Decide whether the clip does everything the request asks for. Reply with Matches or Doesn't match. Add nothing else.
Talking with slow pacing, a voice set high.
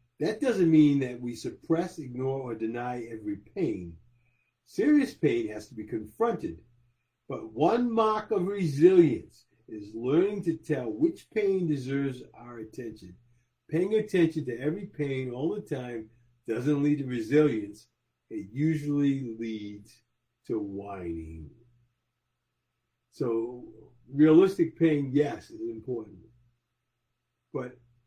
Doesn't match